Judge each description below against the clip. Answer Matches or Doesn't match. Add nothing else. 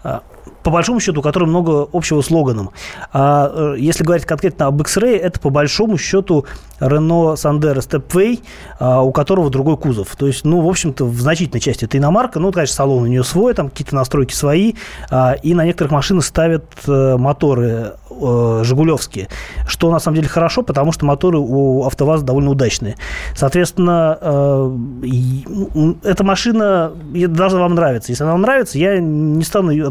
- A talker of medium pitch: Matches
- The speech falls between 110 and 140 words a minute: Doesn't match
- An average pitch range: Matches